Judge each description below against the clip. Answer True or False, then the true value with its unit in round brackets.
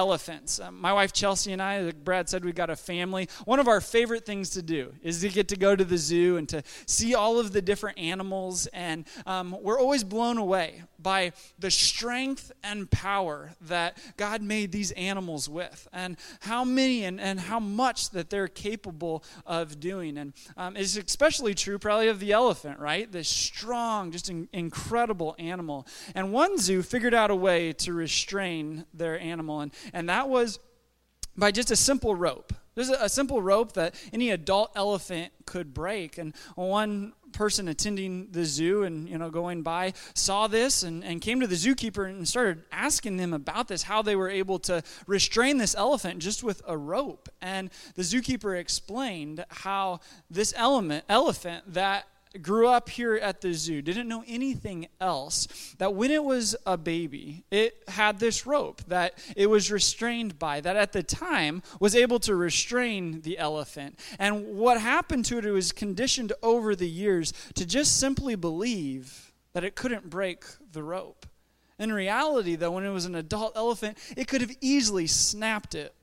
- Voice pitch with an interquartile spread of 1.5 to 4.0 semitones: False (4.4 semitones)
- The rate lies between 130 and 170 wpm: False (180 wpm)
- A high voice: True (195 Hz)